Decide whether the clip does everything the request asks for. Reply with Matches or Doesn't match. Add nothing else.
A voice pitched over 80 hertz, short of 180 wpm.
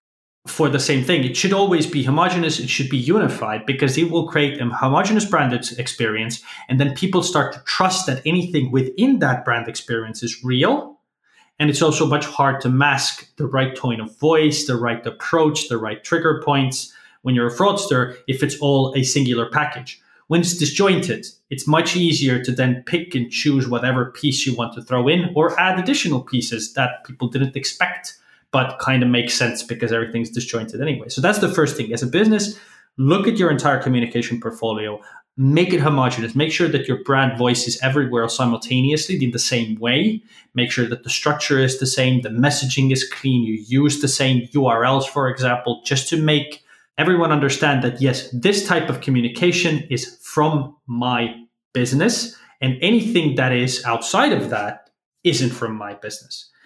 Doesn't match